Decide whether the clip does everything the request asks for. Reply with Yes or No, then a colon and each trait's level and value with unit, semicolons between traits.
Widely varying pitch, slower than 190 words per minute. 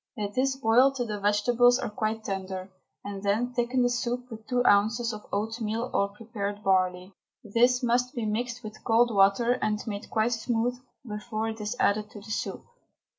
No: average, 2.8 semitones; average, 180 wpm